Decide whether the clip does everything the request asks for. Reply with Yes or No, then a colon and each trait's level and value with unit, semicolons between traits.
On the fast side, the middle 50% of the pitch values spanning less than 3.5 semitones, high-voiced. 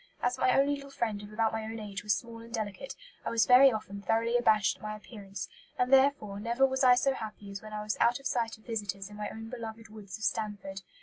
Yes: fast, 250 wpm; narrow, 2.6 semitones; high, 220 Hz